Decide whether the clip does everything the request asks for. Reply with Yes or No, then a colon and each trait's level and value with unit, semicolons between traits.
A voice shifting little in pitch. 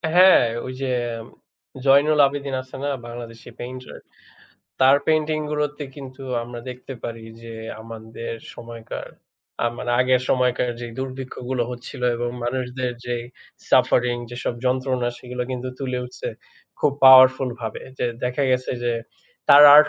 Yes: narrow, 1.7 semitones